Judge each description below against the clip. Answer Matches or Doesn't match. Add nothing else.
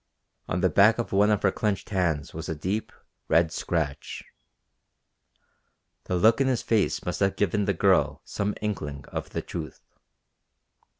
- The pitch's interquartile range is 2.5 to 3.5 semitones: Doesn't match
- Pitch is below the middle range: Matches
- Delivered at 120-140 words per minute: Doesn't match